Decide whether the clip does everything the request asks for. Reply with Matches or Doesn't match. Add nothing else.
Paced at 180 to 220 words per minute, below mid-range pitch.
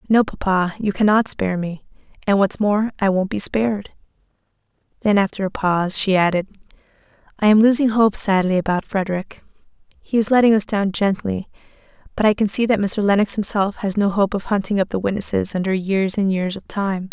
Doesn't match